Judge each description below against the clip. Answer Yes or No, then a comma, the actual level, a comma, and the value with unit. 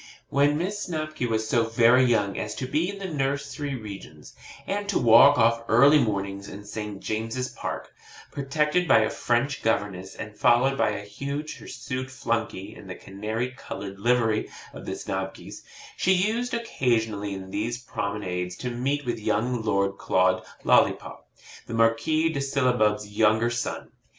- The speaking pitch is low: Yes, low, 115 Hz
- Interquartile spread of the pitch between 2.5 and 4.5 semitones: No, average, 4.9 semitones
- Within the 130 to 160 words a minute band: Yes, average, 155 wpm